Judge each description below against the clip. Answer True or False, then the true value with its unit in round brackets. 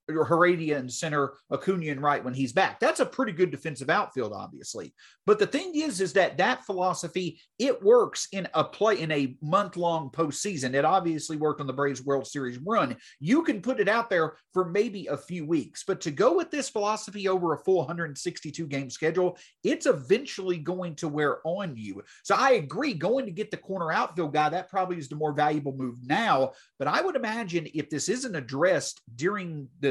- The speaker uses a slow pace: False (205 wpm)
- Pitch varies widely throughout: False (4.7 semitones)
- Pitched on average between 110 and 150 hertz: False (170 Hz)